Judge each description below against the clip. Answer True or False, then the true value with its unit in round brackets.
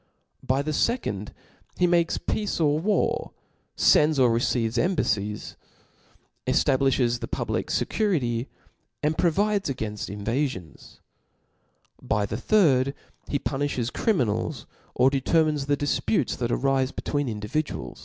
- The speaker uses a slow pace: True (115 wpm)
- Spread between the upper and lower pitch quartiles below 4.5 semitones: False (5.0 semitones)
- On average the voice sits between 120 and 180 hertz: True (135 Hz)